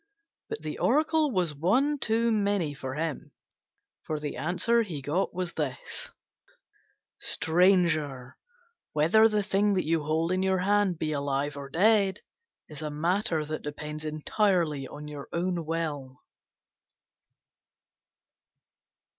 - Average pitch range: Yes, average, 4.8 semitones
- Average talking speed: No, slow, 125 wpm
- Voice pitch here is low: No, medium, 165 Hz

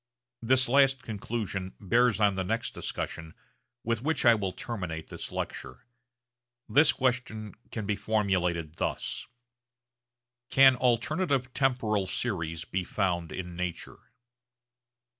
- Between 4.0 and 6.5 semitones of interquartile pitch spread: Yes, average, 5.2 semitones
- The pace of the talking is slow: Yes, slow, 115 wpm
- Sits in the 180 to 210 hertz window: No, low, 110 Hz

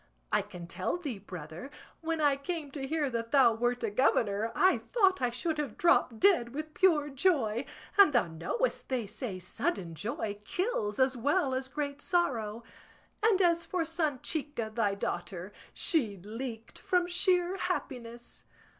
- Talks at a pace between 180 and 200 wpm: No, average, 155 wpm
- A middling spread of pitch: No, wide, 7.0 semitones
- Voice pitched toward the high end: Yes, very high, 265 Hz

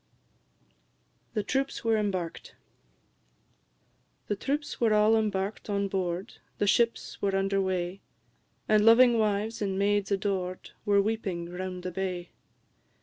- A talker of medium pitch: No, high, 200 Hz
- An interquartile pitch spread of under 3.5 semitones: Yes, narrow, 2.4 semitones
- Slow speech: Yes, slow, 125 wpm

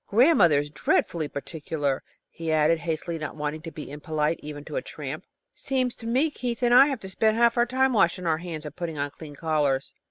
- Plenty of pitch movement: Yes, wide, 7.7 semitones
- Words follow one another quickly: Yes, fast, 215 wpm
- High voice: No, medium, 165 Hz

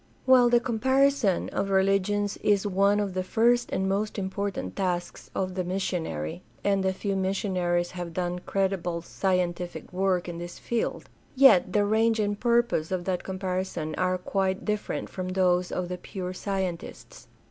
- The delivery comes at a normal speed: Yes, average, 160 wpm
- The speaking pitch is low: No, high, 190 Hz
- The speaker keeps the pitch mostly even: Yes, narrow, 2.2 semitones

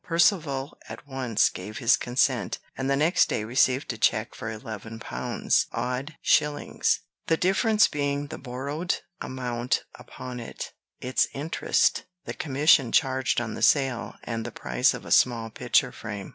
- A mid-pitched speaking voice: No, low, 130 Hz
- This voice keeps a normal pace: Yes, average, 155 wpm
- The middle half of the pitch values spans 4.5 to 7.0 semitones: No, average, 3.9 semitones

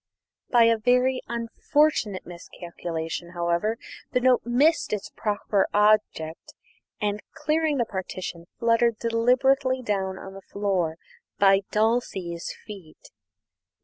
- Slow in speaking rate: Yes, slow, 110 wpm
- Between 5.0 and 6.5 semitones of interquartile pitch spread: No, average, 4.6 semitones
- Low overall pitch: No, high, 215 Hz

